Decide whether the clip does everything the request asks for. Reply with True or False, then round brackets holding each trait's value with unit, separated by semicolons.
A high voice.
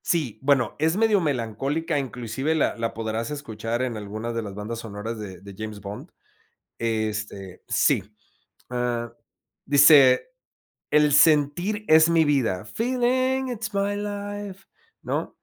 False (135 Hz)